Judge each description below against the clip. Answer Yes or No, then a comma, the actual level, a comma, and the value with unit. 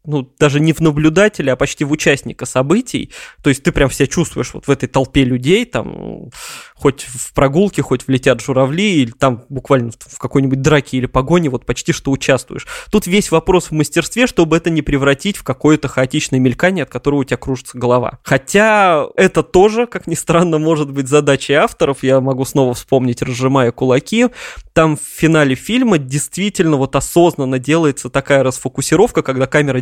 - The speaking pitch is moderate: Yes, medium, 145 Hz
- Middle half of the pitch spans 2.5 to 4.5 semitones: Yes, average, 4.2 semitones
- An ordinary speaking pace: No, fast, 175 wpm